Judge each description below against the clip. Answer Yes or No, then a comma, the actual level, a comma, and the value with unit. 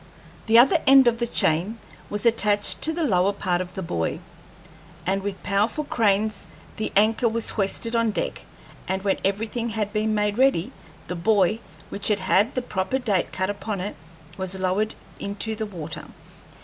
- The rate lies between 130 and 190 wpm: Yes, average, 175 wpm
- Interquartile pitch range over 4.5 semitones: No, average, 3.1 semitones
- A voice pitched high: Yes, high, 210 Hz